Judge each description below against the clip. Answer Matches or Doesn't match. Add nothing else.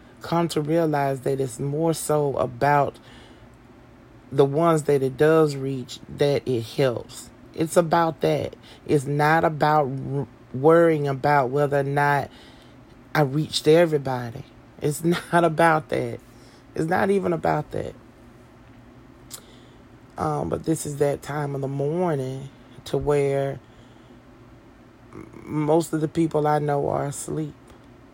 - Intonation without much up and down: Doesn't match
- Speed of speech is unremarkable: Doesn't match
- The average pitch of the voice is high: Doesn't match